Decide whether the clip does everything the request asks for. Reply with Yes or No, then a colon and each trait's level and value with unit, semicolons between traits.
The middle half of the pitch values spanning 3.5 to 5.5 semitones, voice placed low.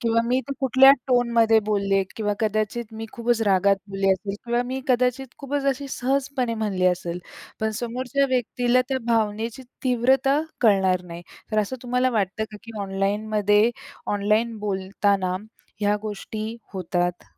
No: average, 3.8 semitones; high, 220 Hz